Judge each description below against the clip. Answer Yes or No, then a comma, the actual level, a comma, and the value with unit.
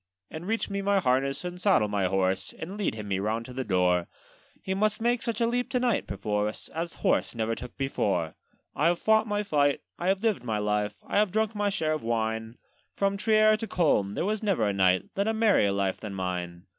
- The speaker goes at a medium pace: No, fast, 225 wpm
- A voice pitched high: No, medium, 145 Hz